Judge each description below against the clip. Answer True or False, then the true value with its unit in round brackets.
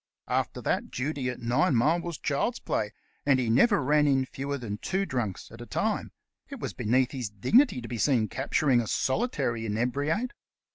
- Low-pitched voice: True (130 Hz)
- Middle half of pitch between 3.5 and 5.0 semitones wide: True (4.2 semitones)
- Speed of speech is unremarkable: True (180 wpm)